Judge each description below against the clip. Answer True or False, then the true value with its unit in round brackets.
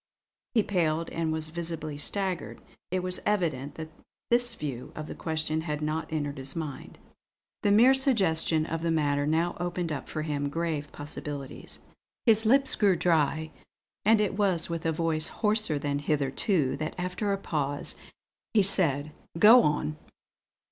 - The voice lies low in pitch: False (160 Hz)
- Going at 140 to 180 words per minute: True (155 wpm)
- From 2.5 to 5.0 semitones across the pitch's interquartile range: True (3.9 semitones)